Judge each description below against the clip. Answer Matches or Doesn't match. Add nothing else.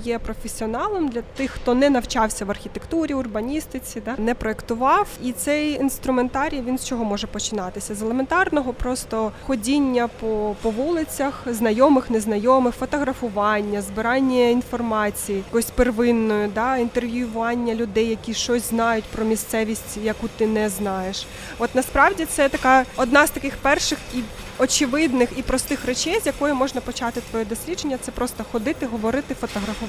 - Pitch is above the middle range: Matches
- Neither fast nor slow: Matches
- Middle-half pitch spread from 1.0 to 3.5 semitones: Matches